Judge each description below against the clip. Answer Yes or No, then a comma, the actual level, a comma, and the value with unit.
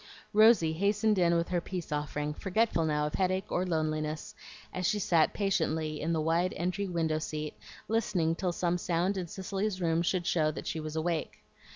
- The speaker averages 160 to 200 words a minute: Yes, average, 185 wpm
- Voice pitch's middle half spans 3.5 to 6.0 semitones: No, average, 3.1 semitones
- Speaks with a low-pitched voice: No, medium, 170 Hz